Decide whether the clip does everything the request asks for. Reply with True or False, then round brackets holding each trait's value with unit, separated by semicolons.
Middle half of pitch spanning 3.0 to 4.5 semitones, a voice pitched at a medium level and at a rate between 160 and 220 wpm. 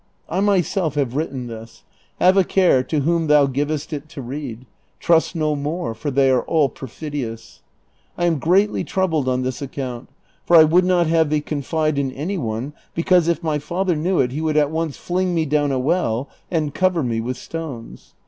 True (4.1 semitones; 150 Hz; 195 wpm)